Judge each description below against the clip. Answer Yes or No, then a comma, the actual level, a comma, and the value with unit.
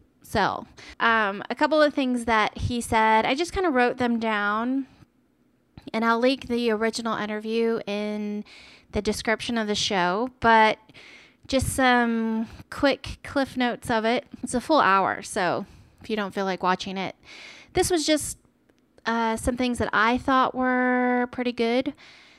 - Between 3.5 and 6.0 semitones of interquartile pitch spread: No, average, 2.8 semitones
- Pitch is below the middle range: No, high, 230 Hz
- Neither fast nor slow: Yes, average, 160 wpm